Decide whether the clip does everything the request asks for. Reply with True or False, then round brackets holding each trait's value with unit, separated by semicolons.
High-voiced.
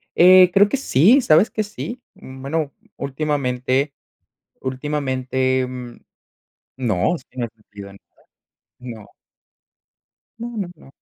False (135 Hz)